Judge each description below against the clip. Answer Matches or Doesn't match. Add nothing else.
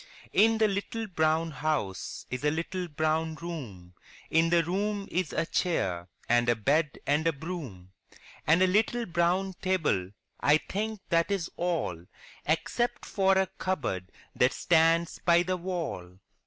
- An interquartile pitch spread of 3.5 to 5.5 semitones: Matches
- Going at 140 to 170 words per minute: Matches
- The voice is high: Doesn't match